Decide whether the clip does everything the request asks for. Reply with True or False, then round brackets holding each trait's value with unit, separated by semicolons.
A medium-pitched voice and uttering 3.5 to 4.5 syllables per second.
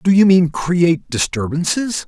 True (170 Hz; 4.4 syllables/s)